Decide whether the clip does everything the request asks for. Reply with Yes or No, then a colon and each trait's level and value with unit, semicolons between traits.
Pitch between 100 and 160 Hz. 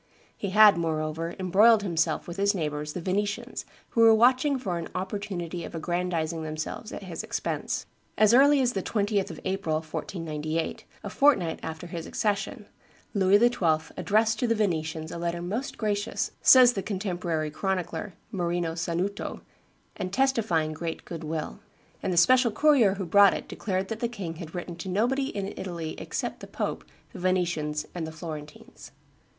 No: medium, 185 Hz